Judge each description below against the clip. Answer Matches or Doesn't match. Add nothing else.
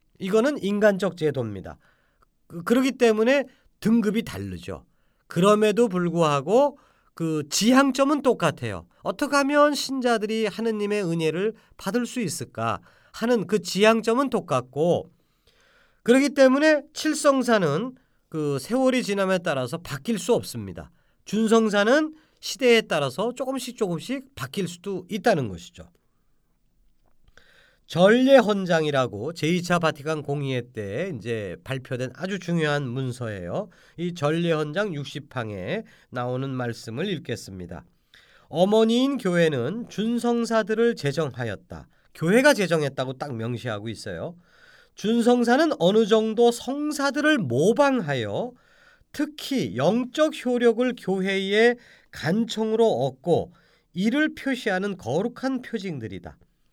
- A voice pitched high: Matches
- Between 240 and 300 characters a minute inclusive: Matches